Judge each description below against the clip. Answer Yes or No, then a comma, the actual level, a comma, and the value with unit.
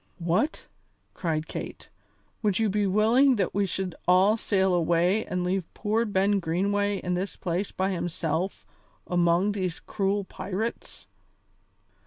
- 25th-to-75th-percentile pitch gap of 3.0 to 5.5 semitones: No, narrow, 2.4 semitones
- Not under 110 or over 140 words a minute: Yes, slow, 135 wpm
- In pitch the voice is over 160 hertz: Yes, high, 190 Hz